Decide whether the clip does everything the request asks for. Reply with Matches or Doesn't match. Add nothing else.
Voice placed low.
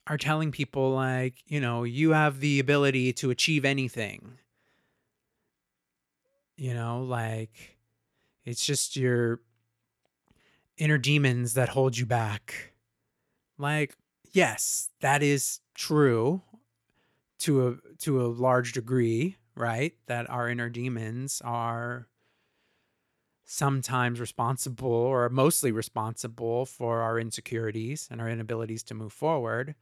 Matches